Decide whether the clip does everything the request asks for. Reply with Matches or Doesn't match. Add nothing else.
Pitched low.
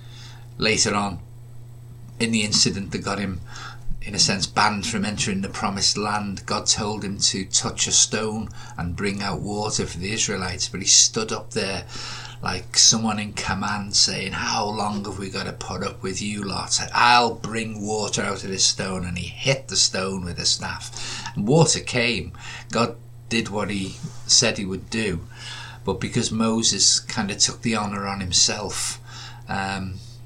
Matches